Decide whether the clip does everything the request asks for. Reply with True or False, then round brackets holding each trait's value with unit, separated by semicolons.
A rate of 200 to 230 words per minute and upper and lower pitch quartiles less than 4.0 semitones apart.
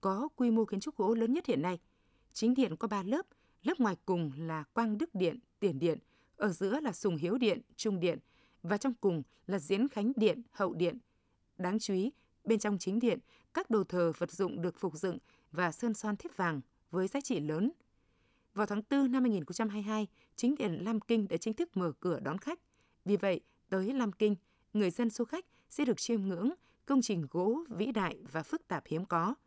False (210 wpm; 4.7 semitones)